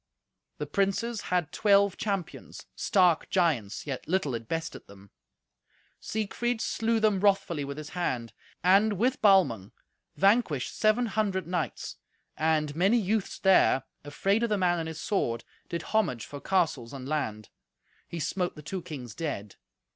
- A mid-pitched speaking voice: Yes, medium, 175 Hz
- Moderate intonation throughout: No, wide, 5.8 semitones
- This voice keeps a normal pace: Yes, average, 145 wpm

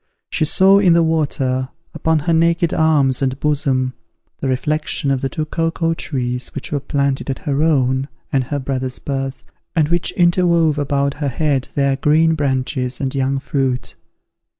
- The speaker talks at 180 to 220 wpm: No, average, 165 wpm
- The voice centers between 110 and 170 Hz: Yes, medium, 140 Hz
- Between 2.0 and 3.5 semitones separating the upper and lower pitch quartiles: Yes, average, 3.2 semitones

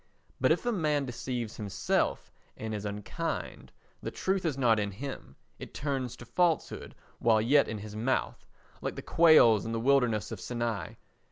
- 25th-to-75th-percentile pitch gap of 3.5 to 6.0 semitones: Yes, average, 4.5 semitones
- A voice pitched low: Yes, low, 120 Hz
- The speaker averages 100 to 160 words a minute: No, average, 170 wpm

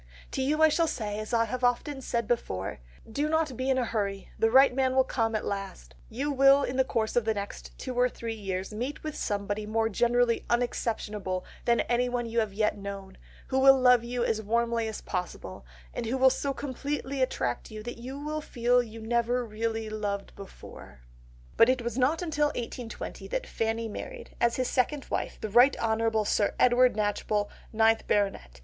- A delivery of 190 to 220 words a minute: Yes, average, 195 wpm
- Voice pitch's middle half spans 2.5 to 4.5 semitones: Yes, average, 3.3 semitones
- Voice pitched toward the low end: No, high, 235 Hz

